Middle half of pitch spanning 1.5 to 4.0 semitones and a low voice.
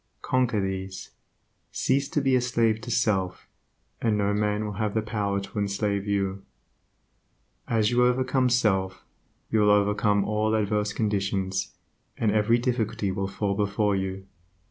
Yes: narrow, 2.4 semitones; low, 105 Hz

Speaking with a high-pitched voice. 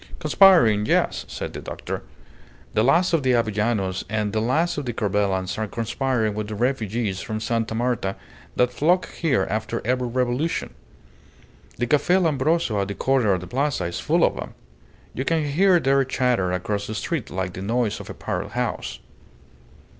No: low, 120 Hz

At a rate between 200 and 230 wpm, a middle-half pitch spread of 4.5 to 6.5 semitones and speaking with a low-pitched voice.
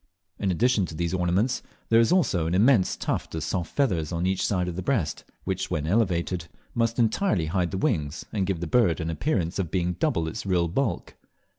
Yes: fast, 205 wpm; average, 4.8 semitones; very low, 90 Hz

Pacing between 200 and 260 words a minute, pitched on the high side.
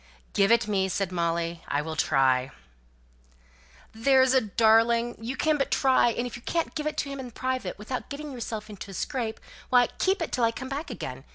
Yes: fast, 205 wpm; high, 235 Hz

